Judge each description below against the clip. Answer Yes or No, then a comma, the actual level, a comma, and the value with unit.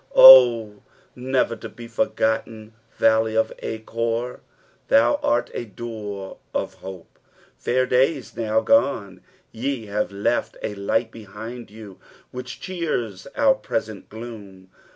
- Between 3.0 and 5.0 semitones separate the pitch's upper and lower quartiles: No, narrow, 2.5 semitones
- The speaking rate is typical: No, slow, 125 wpm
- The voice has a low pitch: Yes, low, 115 Hz